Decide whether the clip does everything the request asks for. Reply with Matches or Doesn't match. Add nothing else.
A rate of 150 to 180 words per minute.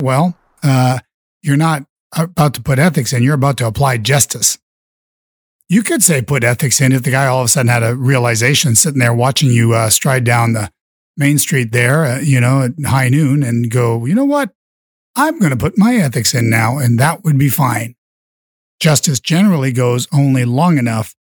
Doesn't match